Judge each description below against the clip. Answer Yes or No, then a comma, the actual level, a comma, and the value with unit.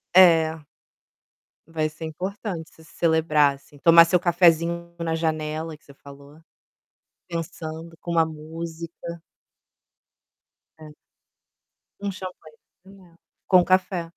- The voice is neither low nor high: Yes, medium, 165 Hz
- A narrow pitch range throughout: Yes, narrow, 1.6 semitones